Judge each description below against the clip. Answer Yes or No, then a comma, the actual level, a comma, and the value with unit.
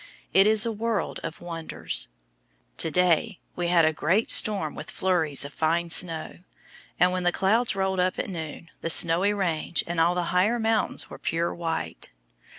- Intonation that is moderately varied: Yes, average, 3.0 semitones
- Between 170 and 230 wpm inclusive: Yes, average, 175 wpm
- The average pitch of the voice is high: No, medium, 175 Hz